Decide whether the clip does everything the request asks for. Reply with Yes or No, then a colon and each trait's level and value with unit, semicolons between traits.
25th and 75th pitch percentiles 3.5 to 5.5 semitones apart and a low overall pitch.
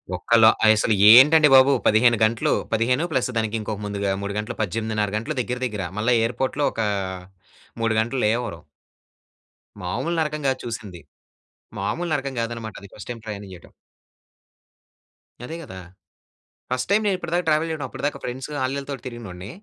Yes: average, 4.4 semitones; low, 120 Hz